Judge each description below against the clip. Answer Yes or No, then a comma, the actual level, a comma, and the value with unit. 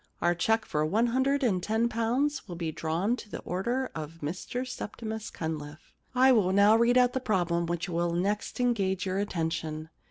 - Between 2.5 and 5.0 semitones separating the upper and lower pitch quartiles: No, wide, 5.6 semitones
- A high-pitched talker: Yes, high, 200 Hz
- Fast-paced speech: No, average, 190 wpm